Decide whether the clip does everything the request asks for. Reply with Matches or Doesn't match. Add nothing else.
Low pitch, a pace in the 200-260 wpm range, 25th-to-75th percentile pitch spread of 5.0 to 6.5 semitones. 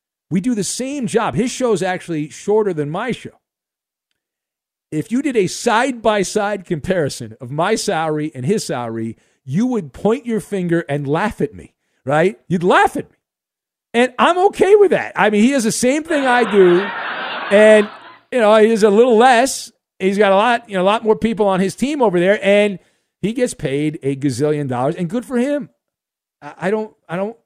Doesn't match